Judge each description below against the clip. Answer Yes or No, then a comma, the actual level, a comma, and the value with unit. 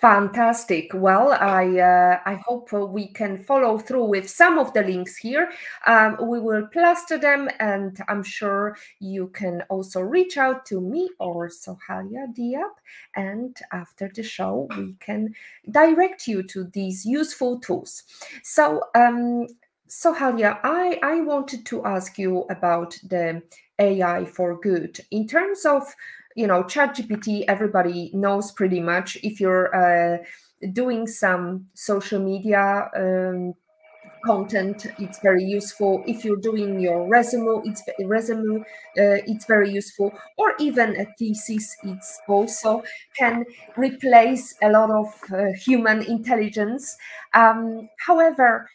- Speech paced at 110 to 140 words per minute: Yes, slow, 135 wpm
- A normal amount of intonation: Yes, average, 3.8 semitones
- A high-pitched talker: Yes, high, 210 Hz